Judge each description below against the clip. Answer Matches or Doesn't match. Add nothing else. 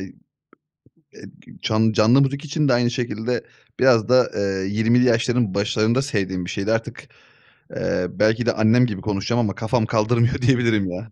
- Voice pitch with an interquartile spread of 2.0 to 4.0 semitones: Matches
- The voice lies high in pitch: Doesn't match